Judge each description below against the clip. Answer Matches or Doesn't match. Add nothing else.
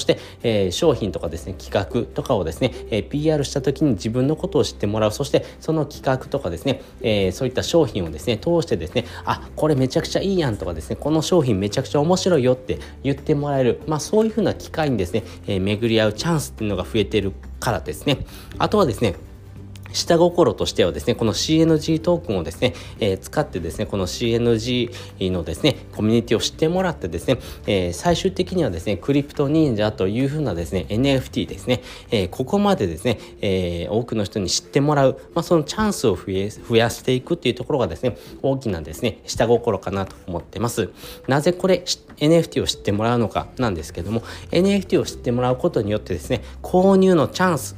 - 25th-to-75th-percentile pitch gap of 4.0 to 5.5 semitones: Doesn't match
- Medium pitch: Doesn't match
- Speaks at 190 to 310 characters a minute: Doesn't match